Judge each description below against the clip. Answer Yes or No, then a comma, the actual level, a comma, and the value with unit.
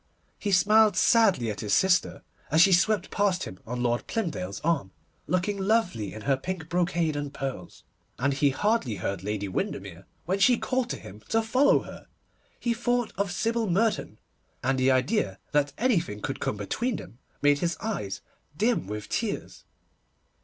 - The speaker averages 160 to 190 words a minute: Yes, average, 165 wpm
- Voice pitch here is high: No, medium, 170 Hz